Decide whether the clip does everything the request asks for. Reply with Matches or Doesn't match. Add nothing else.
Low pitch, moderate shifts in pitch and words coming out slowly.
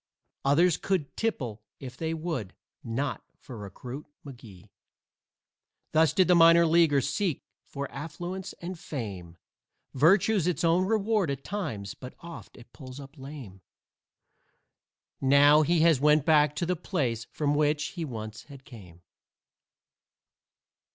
Doesn't match